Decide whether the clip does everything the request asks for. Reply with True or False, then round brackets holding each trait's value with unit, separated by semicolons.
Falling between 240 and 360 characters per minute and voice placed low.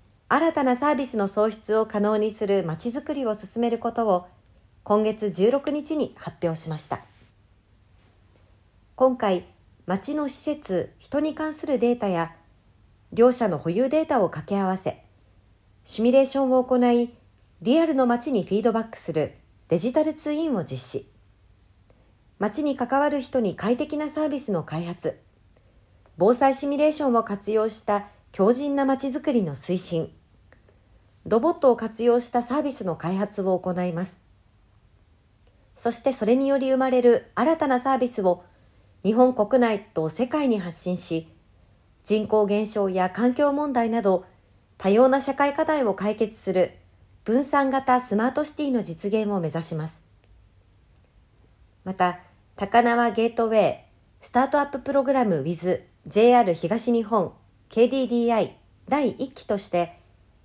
False (280 characters per minute; 210 Hz)